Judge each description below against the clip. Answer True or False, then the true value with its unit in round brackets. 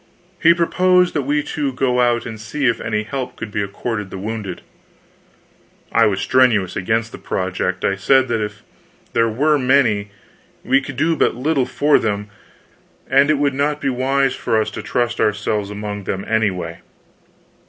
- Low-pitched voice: True (120 Hz)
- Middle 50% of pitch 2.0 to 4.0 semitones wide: False (4.9 semitones)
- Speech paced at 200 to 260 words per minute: False (175 wpm)